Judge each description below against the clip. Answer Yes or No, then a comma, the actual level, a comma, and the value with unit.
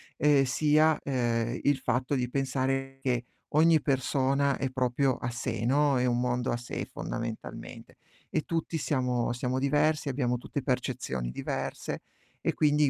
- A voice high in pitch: No, low, 130 Hz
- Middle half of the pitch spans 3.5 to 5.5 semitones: No, average, 2.7 semitones